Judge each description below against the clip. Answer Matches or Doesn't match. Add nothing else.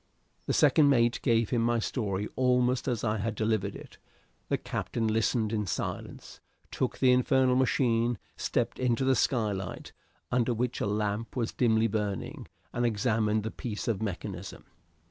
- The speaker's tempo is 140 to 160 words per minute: Matches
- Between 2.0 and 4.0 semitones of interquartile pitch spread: Matches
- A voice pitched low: Matches